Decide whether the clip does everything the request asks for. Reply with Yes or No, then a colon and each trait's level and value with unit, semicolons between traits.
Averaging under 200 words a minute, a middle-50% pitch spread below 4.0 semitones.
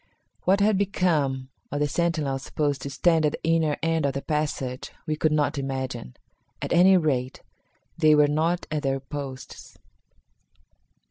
Yes: average, 155 wpm; average, 3.3 semitones